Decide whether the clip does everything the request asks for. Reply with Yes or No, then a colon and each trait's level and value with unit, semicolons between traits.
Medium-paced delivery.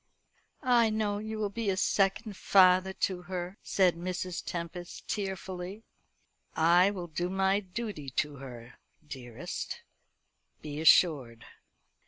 No: slow, 120 wpm